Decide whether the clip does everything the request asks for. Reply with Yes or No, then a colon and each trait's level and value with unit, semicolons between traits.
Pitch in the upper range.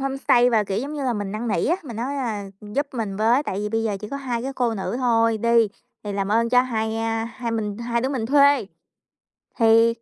Yes: high, 230 Hz